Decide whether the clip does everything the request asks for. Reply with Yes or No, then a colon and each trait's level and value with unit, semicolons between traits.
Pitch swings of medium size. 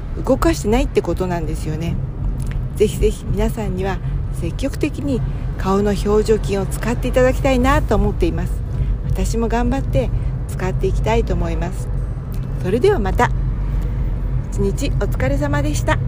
Yes: average, 3.9 semitones